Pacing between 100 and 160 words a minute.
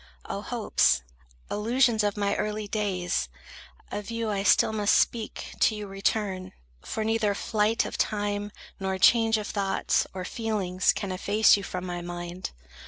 Yes: average, 155 wpm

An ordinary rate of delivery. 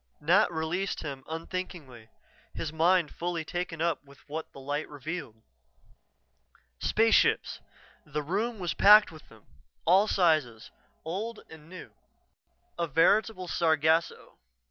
No: slow, 120 wpm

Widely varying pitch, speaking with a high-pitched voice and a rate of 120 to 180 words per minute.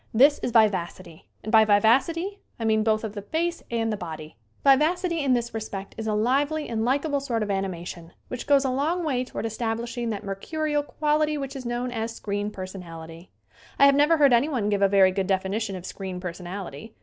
No: wide, 6.1 semitones; high, 225 Hz; average, 195 wpm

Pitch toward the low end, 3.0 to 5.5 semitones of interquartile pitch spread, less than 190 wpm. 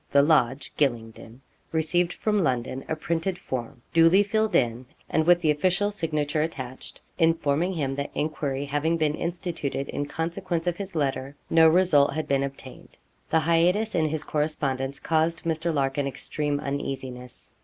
No: medium, 155 Hz; average, 3.4 semitones; average, 155 wpm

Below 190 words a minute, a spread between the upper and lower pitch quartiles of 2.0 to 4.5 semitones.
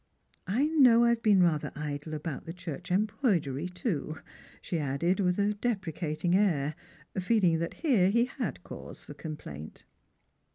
No: average, 155 wpm; wide, 5.6 semitones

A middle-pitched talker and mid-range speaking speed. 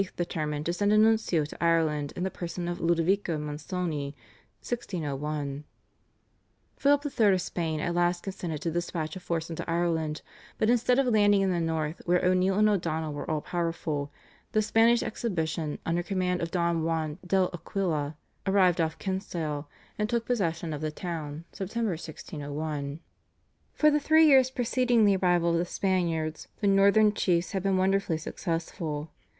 Yes: medium, 175 Hz; average, 160 wpm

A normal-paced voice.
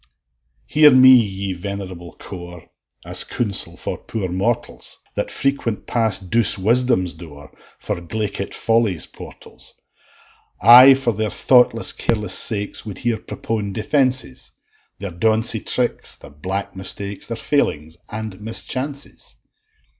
No: slow, 120 wpm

